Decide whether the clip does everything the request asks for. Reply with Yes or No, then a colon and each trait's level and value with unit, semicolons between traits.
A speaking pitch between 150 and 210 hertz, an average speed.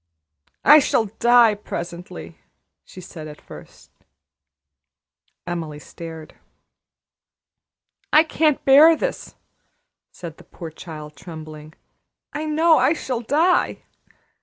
No: medium, 185 Hz; slow, 100 wpm